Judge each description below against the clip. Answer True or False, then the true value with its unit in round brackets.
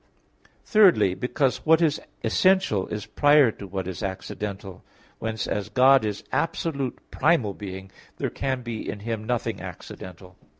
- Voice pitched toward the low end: True (110 Hz)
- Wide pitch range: True (5.8 semitones)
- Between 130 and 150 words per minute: True (140 wpm)